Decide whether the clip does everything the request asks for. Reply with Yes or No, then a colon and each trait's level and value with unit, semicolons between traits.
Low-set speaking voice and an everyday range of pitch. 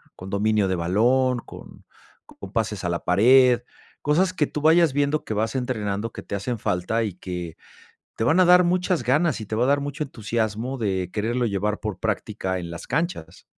No: low, 115 Hz; wide, 5.9 semitones